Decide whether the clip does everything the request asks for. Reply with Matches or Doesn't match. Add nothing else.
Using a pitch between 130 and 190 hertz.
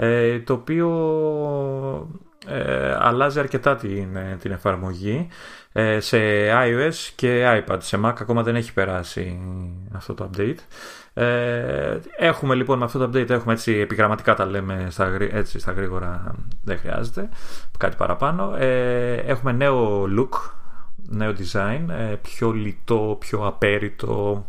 Doesn't match